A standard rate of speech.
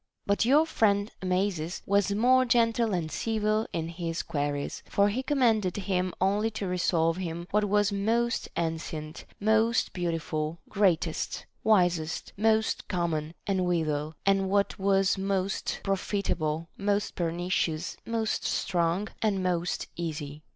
No: slow, 130 wpm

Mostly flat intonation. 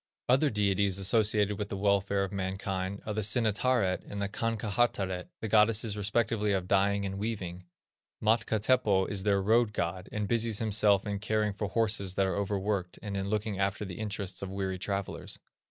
Yes: narrow, 1.8 semitones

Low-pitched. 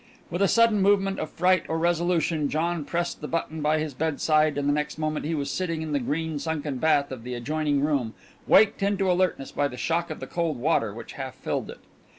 No: medium, 155 Hz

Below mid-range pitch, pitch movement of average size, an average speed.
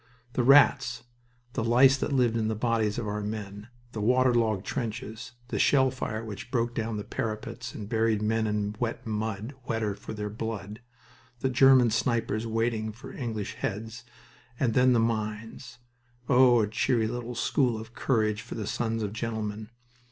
No: low, 115 Hz; narrow, 2.1 semitones; average, 170 wpm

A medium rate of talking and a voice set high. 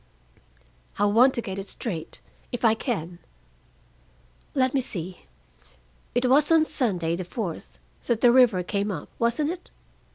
Yes: average, 150 wpm; high, 225 Hz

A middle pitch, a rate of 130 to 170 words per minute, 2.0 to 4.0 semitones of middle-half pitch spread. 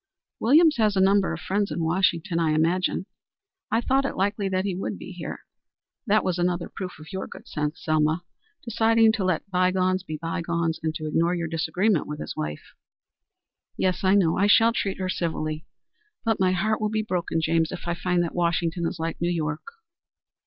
No: medium, 180 Hz; average, 195 wpm; average, 3.3 semitones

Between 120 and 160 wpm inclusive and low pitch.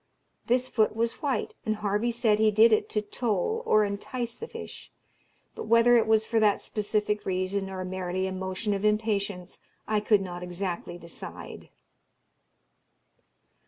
No: average, 155 wpm; high, 210 Hz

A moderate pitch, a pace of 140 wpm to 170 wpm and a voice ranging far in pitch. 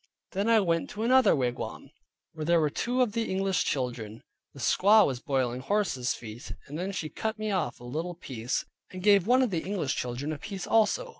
No: medium, 170 Hz; fast, 205 wpm; wide, 8.1 semitones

